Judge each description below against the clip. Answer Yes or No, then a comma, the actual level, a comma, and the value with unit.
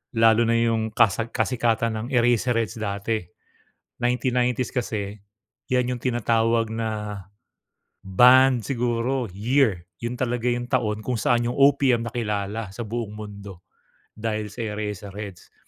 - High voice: No, low, 115 Hz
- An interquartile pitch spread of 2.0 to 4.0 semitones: Yes, narrow, 2.4 semitones